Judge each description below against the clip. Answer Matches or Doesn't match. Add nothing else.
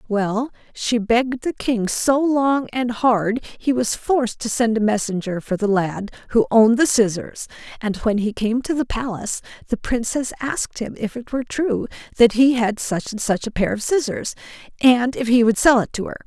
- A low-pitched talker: Doesn't match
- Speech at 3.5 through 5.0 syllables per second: Matches